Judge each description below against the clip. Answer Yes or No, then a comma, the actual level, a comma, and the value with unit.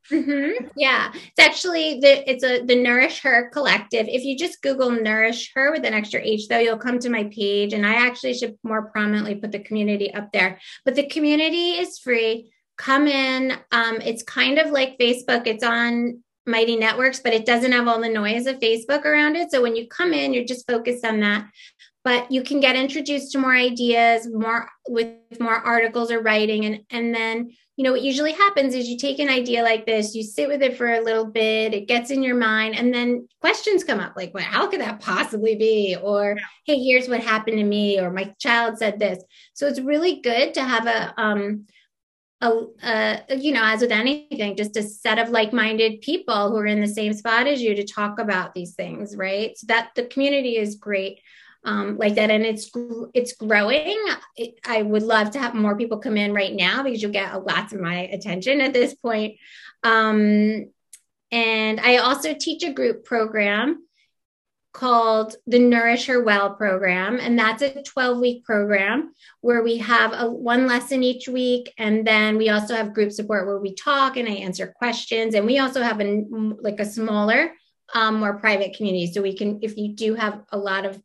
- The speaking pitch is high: Yes, high, 230 Hz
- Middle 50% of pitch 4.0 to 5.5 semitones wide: No, average, 3.1 semitones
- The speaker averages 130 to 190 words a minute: No, fast, 205 wpm